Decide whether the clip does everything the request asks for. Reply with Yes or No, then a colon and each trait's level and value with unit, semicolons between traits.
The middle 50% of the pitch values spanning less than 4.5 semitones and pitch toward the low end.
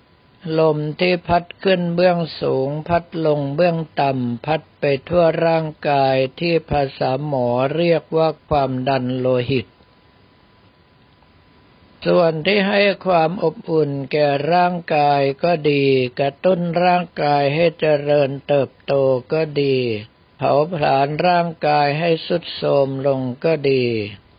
No: average, 3.8 semitones; medium, 150 Hz